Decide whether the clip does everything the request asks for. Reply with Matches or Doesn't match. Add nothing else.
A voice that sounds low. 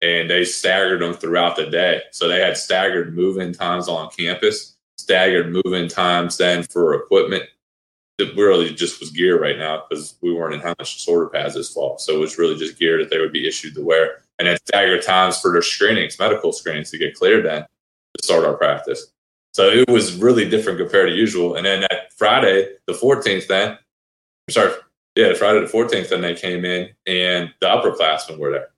Doesn't match